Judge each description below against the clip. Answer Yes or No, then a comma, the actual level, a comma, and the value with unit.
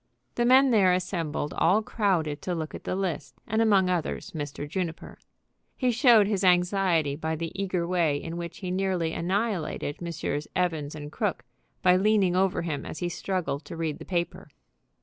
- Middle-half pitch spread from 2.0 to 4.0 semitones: Yes, average, 3.3 semitones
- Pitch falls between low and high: Yes, medium, 180 Hz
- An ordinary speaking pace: Yes, average, 175 wpm